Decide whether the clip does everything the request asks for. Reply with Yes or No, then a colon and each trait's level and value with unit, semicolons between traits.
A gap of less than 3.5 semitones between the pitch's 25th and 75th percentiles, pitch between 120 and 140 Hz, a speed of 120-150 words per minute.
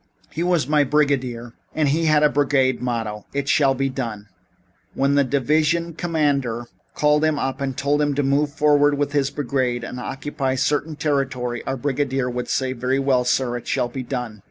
No: narrow, 2.6 semitones; low, 135 Hz; average, 185 wpm